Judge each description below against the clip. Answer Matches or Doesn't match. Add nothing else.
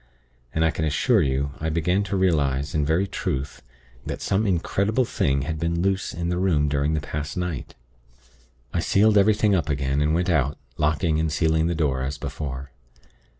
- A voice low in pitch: Matches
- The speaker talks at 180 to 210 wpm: Matches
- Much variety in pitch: Doesn't match